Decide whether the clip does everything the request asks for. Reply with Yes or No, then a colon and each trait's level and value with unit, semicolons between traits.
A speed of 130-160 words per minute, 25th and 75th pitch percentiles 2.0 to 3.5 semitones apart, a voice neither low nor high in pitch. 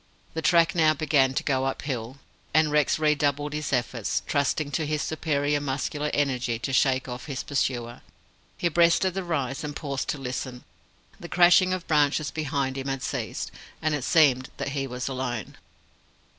No: average, 170 wpm; average, 2.9 semitones; medium, 145 Hz